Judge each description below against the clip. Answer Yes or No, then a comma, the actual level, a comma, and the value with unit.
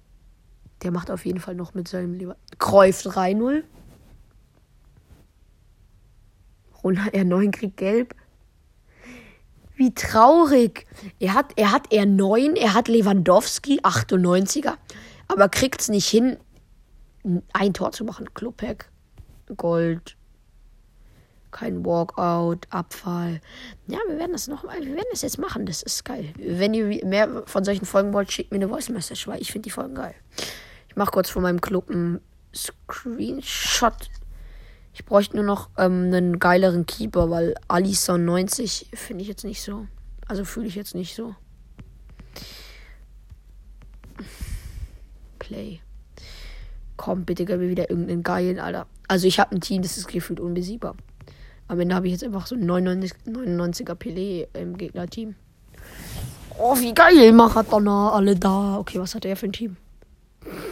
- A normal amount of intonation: Yes, average, 3.5 semitones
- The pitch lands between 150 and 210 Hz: Yes, high, 190 Hz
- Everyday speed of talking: Yes, average, 145 wpm